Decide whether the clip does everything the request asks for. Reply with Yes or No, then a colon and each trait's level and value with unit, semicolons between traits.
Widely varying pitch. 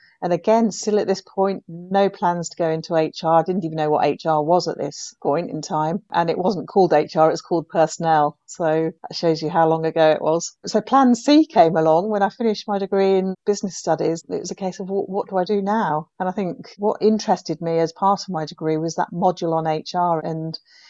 No: average, 3.6 semitones